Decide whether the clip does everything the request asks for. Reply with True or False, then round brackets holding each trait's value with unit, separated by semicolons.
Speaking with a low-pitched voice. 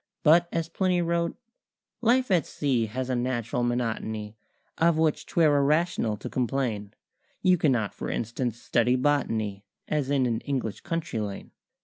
True (130 Hz)